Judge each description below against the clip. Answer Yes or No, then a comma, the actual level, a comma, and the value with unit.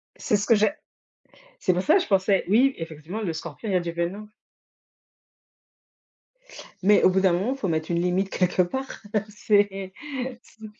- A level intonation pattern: No, average, 3.3 semitones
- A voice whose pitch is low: No, high, 195 Hz